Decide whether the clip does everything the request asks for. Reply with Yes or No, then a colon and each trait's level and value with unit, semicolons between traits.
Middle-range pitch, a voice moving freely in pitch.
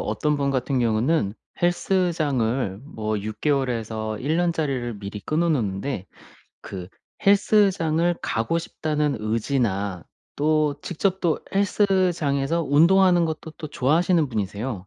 Yes: medium, 145 Hz; wide, 7.2 semitones